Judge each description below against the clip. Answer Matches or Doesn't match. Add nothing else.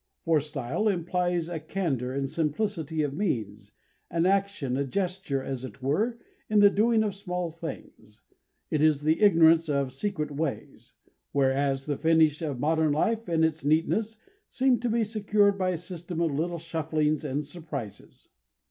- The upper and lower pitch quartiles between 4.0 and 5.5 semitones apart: Matches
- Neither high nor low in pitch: Matches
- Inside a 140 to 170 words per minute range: Matches